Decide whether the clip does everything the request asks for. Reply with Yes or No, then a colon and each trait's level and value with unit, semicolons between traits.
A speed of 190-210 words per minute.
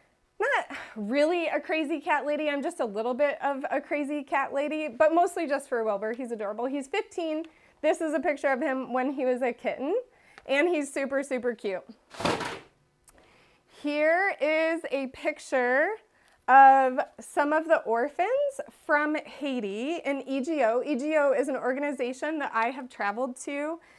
No: average, 160 wpm